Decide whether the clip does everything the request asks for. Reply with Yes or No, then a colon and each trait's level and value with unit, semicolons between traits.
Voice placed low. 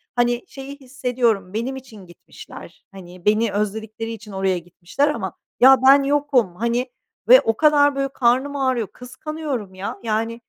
No: high, 235 Hz